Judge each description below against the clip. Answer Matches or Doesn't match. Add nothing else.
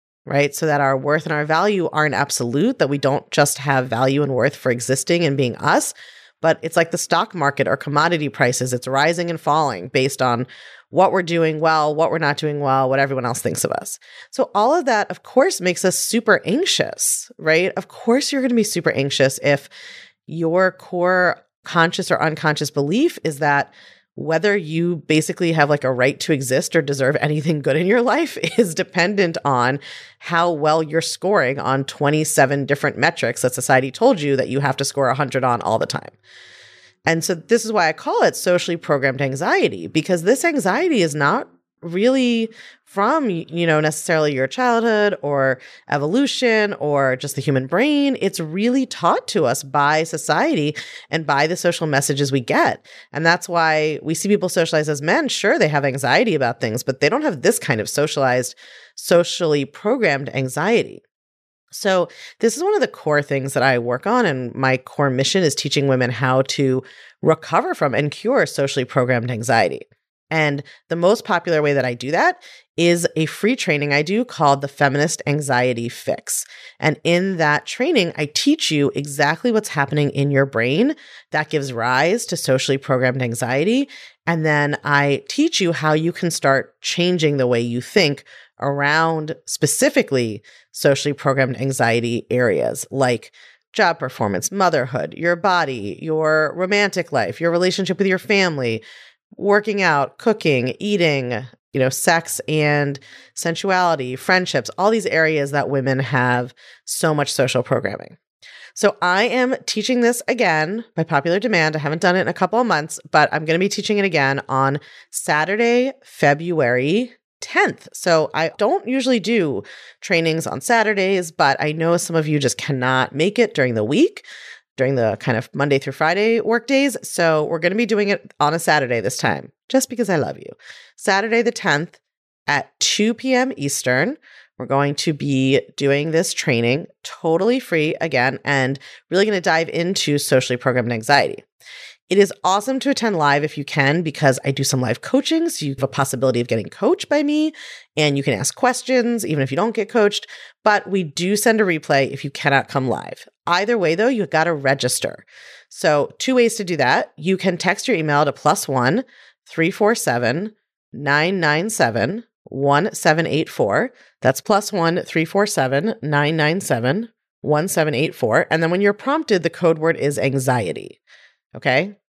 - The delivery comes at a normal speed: Matches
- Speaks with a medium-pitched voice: Matches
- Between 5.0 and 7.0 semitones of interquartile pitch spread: Matches